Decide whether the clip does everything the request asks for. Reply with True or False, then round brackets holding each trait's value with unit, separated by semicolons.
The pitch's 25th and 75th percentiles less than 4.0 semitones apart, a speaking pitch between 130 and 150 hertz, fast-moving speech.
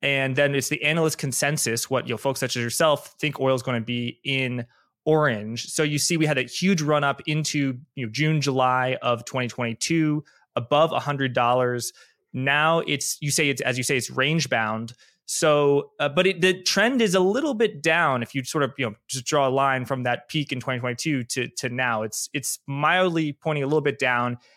True (3.4 semitones; 140 Hz; 215 wpm)